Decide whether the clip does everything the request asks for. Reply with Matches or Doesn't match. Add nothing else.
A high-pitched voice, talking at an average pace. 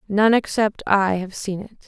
Matches